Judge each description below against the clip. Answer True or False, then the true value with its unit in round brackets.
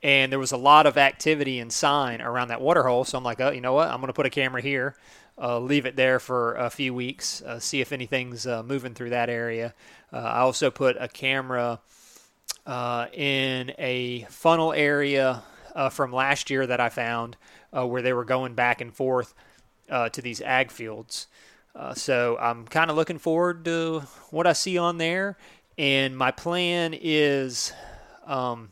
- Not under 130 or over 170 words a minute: False (195 wpm)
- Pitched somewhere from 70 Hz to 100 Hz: False (130 Hz)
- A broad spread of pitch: False (2.8 semitones)